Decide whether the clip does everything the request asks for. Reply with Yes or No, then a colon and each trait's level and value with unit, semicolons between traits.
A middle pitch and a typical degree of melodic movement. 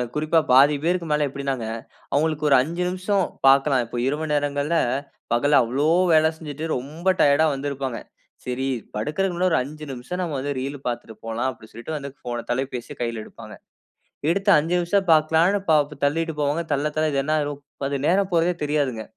Yes: medium, 145 Hz; average, 3.3 semitones